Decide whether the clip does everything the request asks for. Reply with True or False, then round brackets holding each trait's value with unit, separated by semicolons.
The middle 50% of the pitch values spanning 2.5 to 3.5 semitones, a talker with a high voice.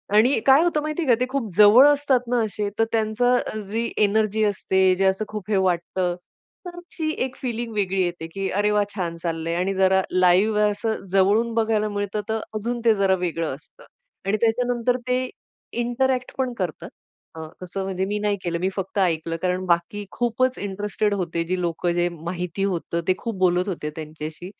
False (4.0 semitones; 205 Hz)